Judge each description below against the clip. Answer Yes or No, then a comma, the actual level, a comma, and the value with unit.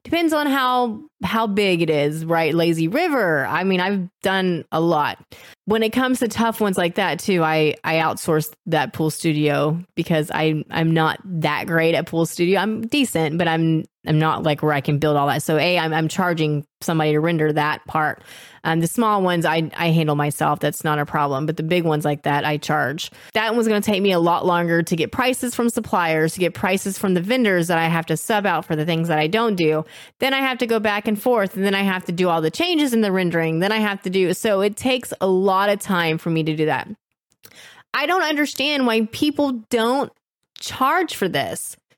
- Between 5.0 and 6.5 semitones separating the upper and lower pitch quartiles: Yes, wide, 5.4 semitones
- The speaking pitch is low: No, medium, 175 Hz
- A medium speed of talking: No, fast, 235 wpm